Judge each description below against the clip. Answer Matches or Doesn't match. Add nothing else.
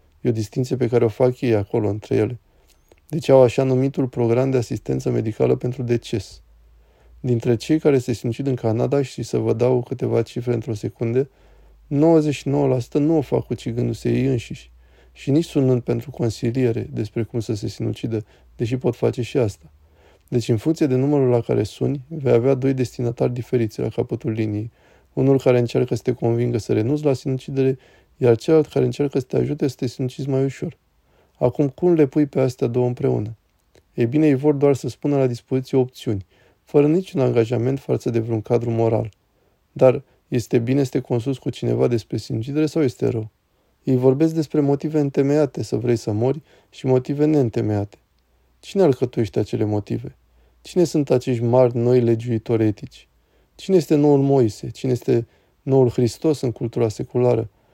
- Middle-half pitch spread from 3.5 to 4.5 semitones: Doesn't match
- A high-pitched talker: Doesn't match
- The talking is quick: Matches